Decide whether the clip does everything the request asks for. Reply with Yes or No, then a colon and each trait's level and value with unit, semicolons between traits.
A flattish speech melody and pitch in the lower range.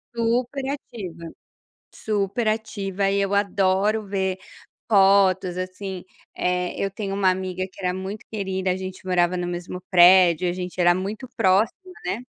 No: narrow, 1.9 semitones; high, 190 Hz